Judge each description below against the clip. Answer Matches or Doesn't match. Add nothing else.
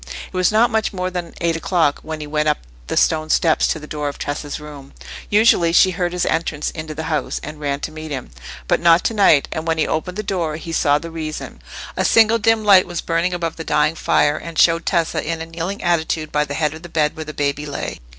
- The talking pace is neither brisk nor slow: Doesn't match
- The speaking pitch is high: Doesn't match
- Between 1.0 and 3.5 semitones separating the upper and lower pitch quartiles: Matches